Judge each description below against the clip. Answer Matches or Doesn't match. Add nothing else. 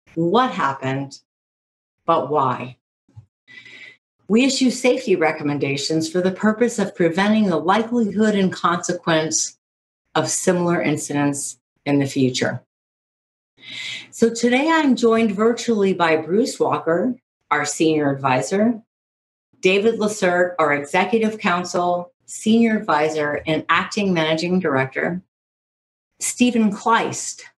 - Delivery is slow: Matches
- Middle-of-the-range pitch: Matches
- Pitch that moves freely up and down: Matches